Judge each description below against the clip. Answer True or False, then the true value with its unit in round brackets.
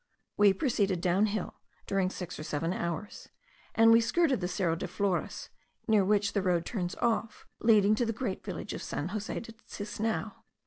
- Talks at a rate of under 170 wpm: False (180 wpm)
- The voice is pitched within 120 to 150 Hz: False (200 Hz)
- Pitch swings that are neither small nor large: True (3.5 semitones)